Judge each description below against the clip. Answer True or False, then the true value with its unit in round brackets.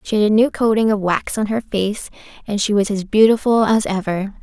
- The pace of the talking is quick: True (230 wpm)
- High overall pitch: True (210 Hz)